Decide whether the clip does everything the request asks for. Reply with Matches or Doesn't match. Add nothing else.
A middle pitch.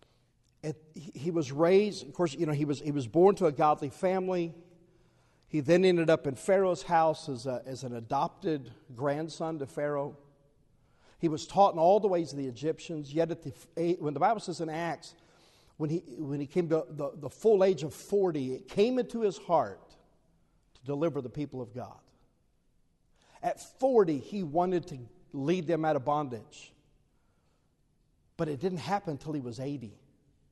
Matches